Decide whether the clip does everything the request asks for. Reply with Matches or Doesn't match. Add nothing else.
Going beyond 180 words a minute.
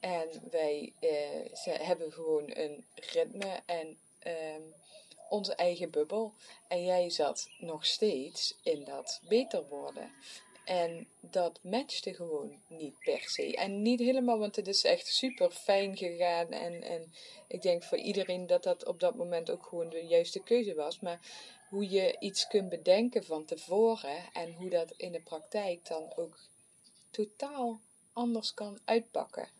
Doesn't match